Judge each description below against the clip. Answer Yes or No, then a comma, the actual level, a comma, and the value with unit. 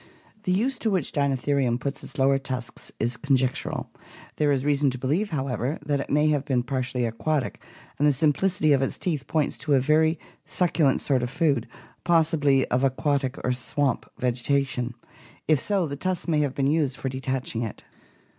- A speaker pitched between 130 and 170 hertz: Yes, medium, 140 Hz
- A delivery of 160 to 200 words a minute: Yes, average, 180 wpm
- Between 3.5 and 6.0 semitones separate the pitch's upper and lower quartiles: No, average, 2.9 semitones